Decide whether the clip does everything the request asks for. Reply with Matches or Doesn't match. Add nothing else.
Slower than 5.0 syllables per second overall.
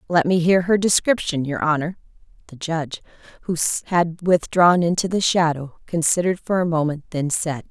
Doesn't match